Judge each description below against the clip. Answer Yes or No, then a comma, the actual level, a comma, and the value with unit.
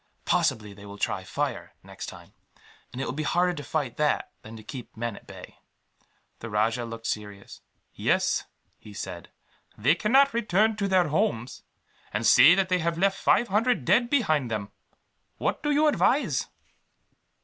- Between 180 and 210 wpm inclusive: No, average, 170 wpm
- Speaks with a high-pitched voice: No, medium, 150 Hz